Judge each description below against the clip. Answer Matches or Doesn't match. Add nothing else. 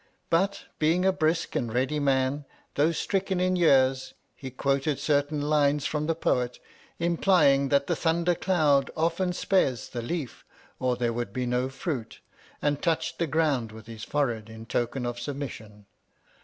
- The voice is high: Doesn't match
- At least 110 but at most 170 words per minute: Matches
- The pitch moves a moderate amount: Matches